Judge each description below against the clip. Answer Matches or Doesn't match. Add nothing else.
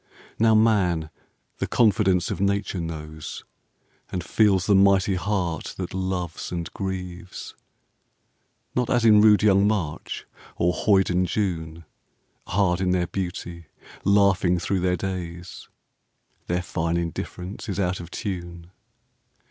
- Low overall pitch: Matches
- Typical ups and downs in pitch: Doesn't match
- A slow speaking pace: Matches